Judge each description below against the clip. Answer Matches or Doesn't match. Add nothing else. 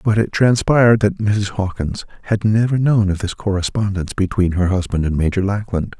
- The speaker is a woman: Doesn't match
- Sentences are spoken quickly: Doesn't match